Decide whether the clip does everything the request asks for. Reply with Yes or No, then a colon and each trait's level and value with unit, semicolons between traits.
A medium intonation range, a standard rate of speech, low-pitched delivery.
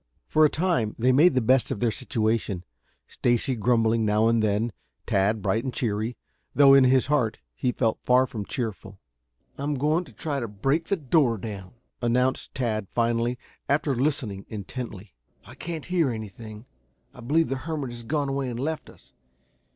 Yes: average, 4.0 semitones; average, 175 wpm; low, 120 Hz